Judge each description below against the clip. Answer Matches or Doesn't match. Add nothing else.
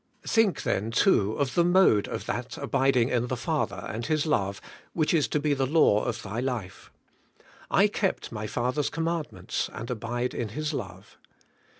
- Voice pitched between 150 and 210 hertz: Doesn't match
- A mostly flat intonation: Doesn't match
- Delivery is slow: Doesn't match